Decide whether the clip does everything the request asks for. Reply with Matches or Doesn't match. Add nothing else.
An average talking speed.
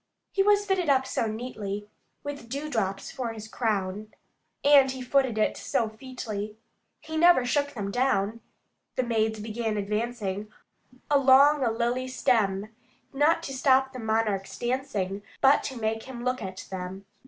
Matches